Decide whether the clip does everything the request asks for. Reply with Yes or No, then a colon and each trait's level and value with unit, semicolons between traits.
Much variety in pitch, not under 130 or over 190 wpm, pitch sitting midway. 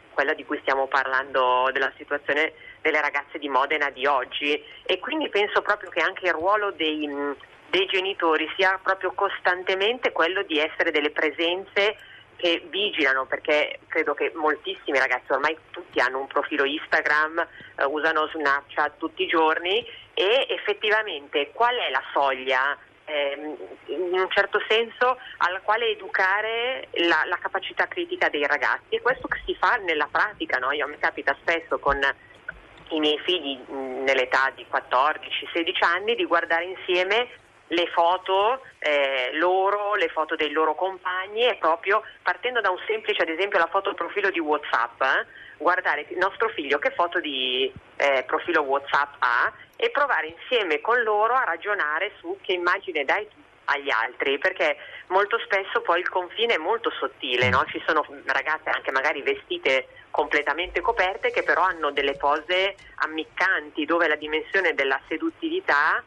Yes: wide, 6.5 semitones; average, 155 wpm; medium, 180 Hz